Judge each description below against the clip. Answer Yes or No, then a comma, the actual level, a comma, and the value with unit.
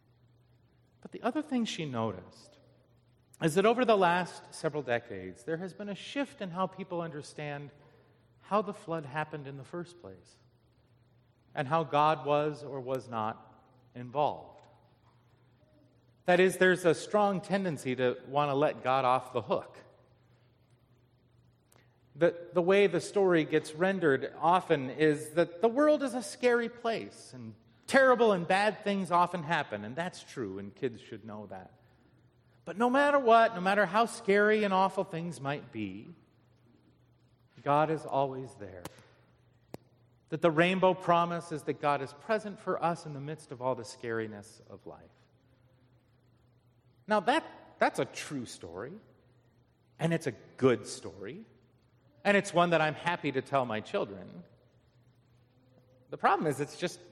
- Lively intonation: Yes, wide, 6.3 semitones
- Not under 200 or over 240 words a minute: No, average, 155 wpm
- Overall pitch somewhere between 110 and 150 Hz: Yes, medium, 145 Hz